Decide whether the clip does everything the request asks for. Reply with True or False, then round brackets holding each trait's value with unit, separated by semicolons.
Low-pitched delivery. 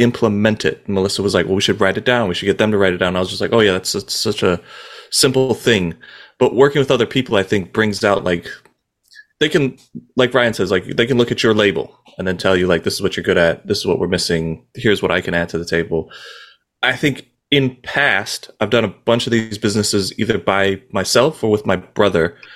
True (100 Hz)